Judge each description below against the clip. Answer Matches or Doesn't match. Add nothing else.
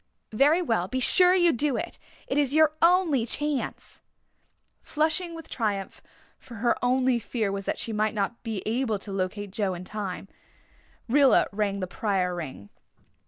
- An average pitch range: Doesn't match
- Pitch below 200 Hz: Doesn't match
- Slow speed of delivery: Doesn't match